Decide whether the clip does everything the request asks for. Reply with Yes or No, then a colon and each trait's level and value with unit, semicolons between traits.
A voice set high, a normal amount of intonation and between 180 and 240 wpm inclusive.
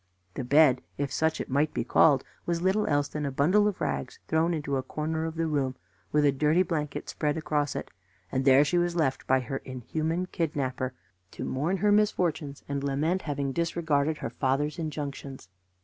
No: medium, 150 Hz; average, 3.0 semitones; average, 190 wpm